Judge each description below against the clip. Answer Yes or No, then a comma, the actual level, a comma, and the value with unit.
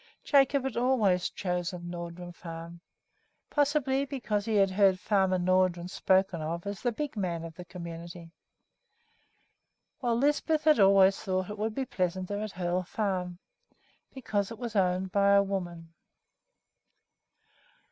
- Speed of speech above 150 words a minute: No, average, 140 wpm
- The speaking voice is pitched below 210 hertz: Yes, high, 190 Hz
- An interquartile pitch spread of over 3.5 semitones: Yes, average, 3.9 semitones